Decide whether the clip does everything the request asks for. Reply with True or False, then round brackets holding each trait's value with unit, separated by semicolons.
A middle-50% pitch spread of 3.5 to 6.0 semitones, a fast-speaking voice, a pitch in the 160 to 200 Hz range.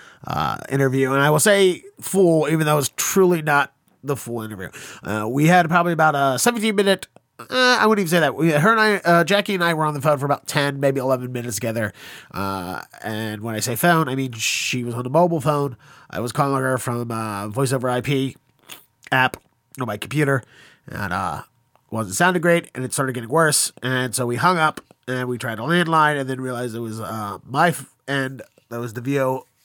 False (5.0 semitones; 220 wpm; 135 Hz)